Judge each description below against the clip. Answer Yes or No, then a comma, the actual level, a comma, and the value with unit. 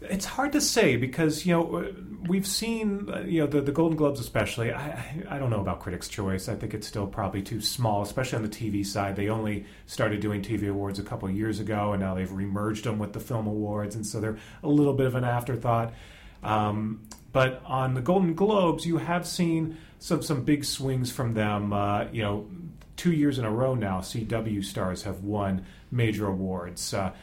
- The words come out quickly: Yes, fast, 210 wpm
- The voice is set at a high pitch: No, low, 110 Hz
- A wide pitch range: Yes, wide, 6.3 semitones